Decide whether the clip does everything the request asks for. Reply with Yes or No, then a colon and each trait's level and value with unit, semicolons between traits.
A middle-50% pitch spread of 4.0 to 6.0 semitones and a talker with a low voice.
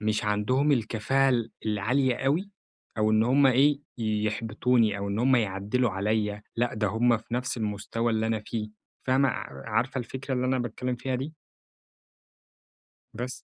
No: average, 3.2 semitones; low, 115 Hz